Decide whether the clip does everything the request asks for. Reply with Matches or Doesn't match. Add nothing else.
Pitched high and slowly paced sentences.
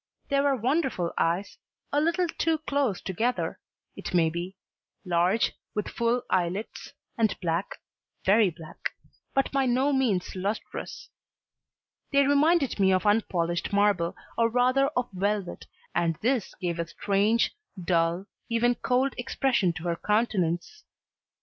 Matches